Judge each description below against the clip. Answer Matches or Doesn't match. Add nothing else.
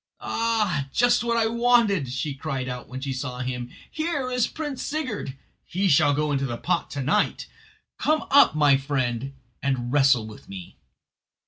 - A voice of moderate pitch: Matches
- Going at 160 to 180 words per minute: Matches